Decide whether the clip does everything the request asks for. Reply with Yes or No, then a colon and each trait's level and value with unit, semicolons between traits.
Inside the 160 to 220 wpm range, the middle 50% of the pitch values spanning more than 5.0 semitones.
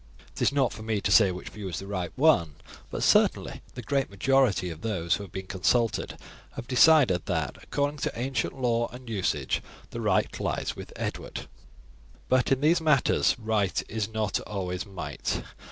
Yes: average, 180 wpm; wide, 5.5 semitones